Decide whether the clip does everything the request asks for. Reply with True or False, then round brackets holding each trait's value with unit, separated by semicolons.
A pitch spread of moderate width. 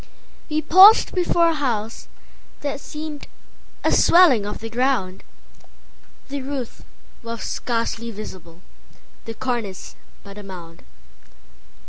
False (6.0 semitones)